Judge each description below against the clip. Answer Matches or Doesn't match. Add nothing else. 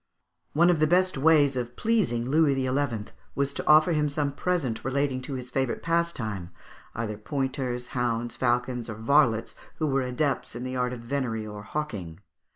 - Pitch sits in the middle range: Doesn't match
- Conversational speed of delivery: Matches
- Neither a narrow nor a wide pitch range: Matches